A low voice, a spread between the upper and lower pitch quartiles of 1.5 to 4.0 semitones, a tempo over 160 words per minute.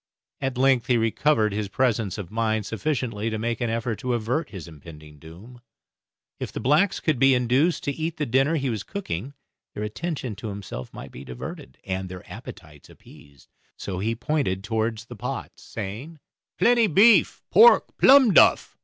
No: low, 115 Hz; wide, 5.6 semitones; average, 170 wpm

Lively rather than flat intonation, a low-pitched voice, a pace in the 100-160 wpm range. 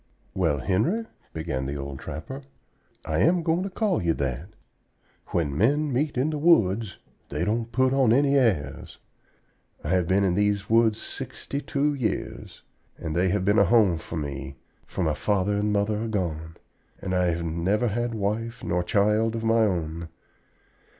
No: wide, 6.0 semitones; low, 100 Hz; average, 170 wpm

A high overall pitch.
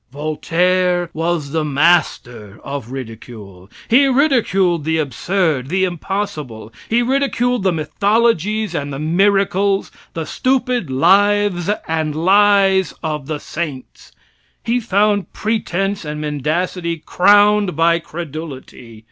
No: medium, 175 Hz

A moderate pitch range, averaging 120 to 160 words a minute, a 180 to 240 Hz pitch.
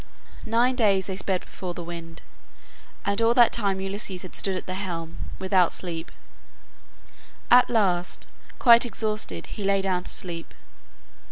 Yes: average, 3.2 semitones; average, 150 wpm; high, 190 Hz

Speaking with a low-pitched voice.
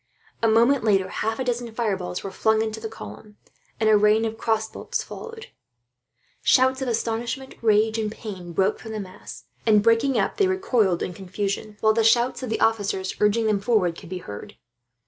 No: high, 220 Hz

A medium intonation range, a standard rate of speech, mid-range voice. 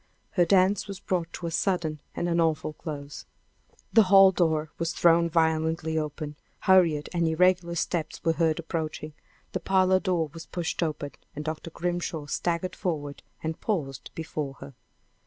No: narrow, 2.3 semitones; average, 155 wpm; medium, 165 Hz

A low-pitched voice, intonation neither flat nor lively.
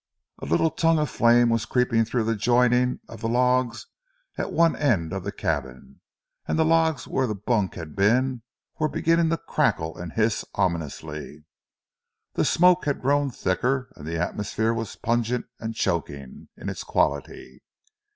No: low, 115 Hz; wide, 6.1 semitones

